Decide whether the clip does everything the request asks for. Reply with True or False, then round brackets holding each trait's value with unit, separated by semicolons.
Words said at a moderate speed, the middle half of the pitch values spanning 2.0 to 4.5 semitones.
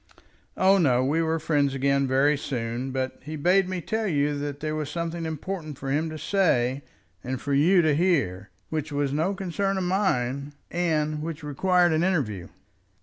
True (180 wpm; 4.0 semitones)